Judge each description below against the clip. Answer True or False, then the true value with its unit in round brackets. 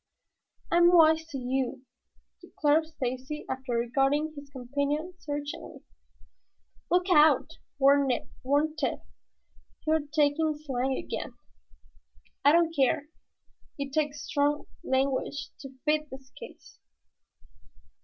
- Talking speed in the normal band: False (105 wpm)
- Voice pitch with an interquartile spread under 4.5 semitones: True (2.6 semitones)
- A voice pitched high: True (290 Hz)